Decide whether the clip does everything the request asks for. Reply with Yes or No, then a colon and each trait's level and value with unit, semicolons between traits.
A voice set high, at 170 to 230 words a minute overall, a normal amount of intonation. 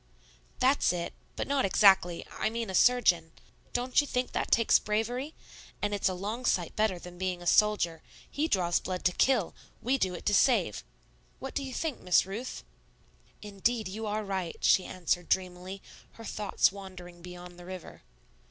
Yes: high, 195 Hz; average, 175 wpm; average, 4.6 semitones